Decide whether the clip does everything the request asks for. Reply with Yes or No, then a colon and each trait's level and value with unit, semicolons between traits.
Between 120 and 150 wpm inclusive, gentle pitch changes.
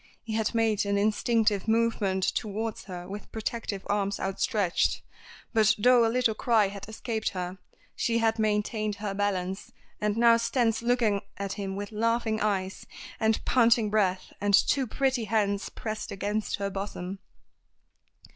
Yes: average, 145 wpm; narrow, 2.2 semitones